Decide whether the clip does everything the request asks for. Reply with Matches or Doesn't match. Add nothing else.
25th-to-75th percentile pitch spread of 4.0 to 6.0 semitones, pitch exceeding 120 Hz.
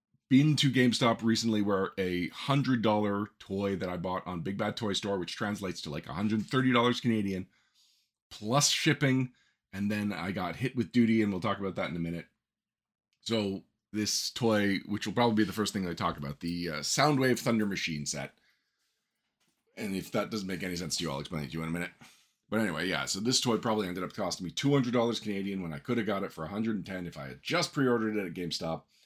Doesn't match